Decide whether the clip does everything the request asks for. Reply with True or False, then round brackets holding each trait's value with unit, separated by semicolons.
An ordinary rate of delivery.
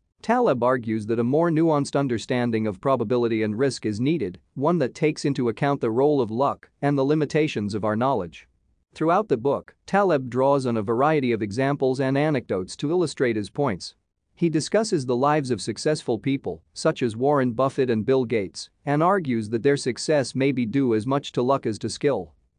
True (195 wpm)